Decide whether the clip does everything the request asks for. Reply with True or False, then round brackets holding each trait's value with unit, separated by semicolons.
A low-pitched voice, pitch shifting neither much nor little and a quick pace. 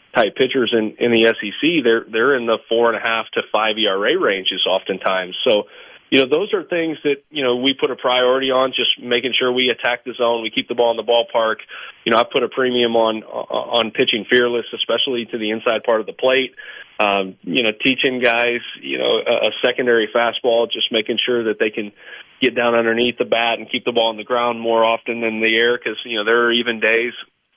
False (120 Hz; 2.1 semitones; 230 wpm)